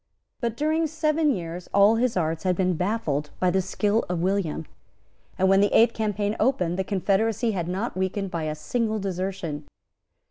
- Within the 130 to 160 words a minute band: No, average, 180 wpm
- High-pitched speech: Yes, high, 195 Hz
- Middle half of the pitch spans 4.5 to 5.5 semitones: No, average, 3.9 semitones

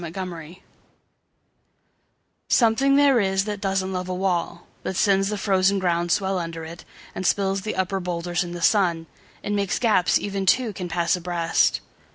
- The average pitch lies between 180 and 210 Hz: Yes, high, 190 Hz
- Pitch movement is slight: Yes, narrow, 2.3 semitones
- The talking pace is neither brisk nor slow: Yes, average, 155 wpm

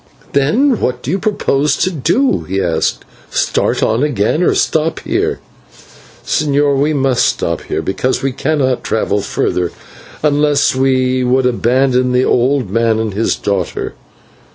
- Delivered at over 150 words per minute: No, average, 145 wpm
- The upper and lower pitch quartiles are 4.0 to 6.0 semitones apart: No, average, 3.6 semitones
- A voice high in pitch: No, low, 130 Hz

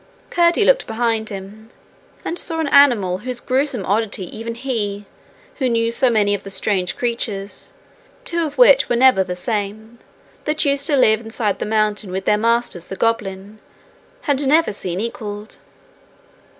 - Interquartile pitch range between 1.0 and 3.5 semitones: No, average, 4.2 semitones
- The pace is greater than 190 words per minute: No, average, 160 wpm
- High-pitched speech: Yes, high, 225 Hz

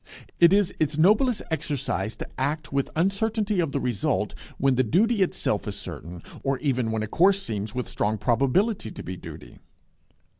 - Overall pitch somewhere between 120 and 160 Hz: Yes, medium, 140 Hz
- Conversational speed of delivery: Yes, average, 175 wpm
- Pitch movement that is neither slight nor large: No, wide, 8.4 semitones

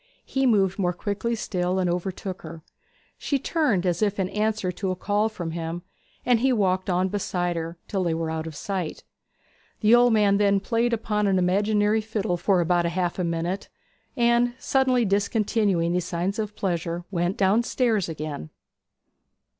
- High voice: Yes, high, 195 Hz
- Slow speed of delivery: No, average, 170 wpm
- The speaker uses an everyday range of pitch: Yes, average, 3.6 semitones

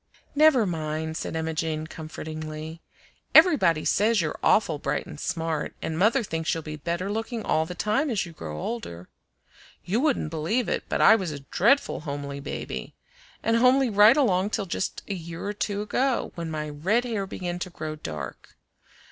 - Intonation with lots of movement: Yes, wide, 5.8 semitones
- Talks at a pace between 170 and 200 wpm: Yes, average, 180 wpm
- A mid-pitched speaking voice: Yes, medium, 170 Hz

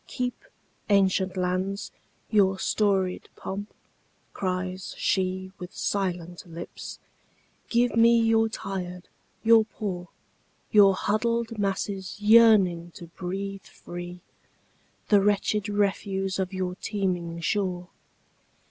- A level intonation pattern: Yes, narrow, 2.3 semitones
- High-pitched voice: Yes, high, 195 Hz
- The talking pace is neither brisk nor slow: No, slow, 90 wpm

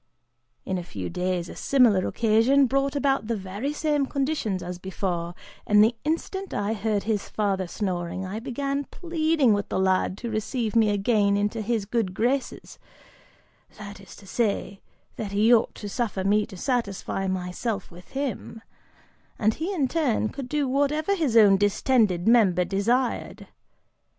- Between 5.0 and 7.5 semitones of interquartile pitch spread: Yes, wide, 5.4 semitones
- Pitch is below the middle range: No, high, 215 Hz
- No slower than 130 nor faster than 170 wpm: Yes, average, 160 wpm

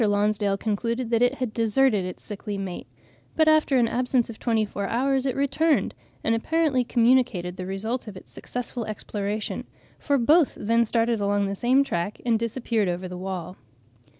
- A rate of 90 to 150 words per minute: No, average, 175 wpm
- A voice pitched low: No, high, 230 Hz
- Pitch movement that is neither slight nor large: Yes, average, 3.9 semitones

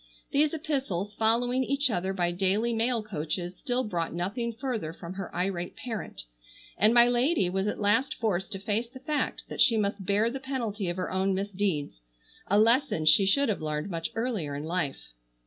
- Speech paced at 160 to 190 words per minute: Yes, average, 185 wpm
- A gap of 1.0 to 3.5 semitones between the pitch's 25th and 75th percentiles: No, average, 5.1 semitones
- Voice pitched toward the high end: Yes, high, 205 Hz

